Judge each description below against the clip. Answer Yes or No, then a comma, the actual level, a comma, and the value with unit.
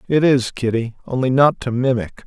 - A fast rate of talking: No, average, 185 wpm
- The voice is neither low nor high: No, low, 125 Hz